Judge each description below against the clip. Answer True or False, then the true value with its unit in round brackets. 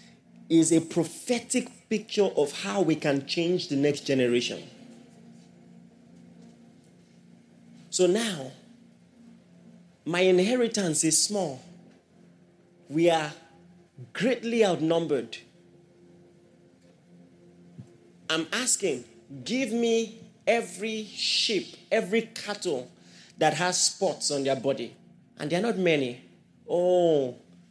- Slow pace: True (90 wpm)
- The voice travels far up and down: True (7.5 semitones)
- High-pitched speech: False (175 Hz)